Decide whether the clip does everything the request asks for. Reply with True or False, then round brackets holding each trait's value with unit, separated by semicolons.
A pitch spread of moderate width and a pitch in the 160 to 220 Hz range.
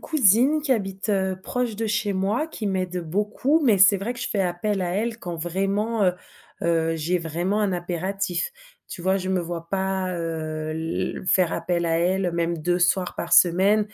True (3.2 semitones; 190 Hz)